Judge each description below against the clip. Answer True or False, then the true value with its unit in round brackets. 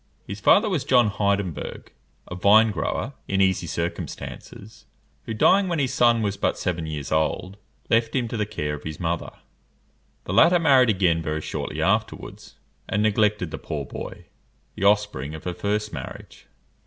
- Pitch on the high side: False (100 Hz)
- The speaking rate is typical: True (165 wpm)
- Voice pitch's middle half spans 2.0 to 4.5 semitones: False (5.1 semitones)